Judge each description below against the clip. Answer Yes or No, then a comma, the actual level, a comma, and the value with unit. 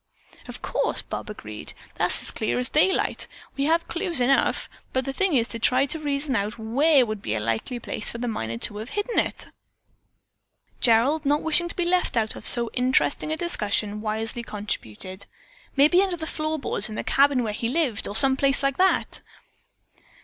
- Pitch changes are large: Yes, wide, 6.0 semitones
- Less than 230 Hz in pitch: No, very high, 260 Hz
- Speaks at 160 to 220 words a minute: Yes, average, 195 wpm